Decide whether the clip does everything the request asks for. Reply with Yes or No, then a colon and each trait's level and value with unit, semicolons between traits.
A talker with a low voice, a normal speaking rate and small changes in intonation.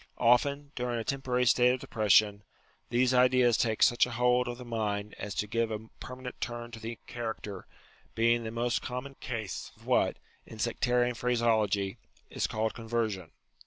Yes: low, 120 Hz; average, 170 wpm; narrow, 1.9 semitones